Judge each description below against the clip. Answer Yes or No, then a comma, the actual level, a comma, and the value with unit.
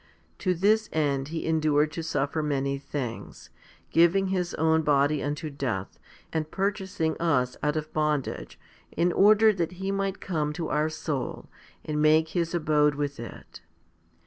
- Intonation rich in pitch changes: No, average, 2.9 semitones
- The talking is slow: No, average, 155 wpm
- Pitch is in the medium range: Yes, medium, 155 Hz